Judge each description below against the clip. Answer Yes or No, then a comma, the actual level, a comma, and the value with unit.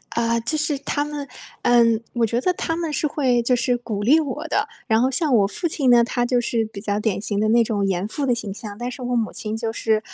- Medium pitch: No, high, 240 Hz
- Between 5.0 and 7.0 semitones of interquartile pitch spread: No, average, 4.1 semitones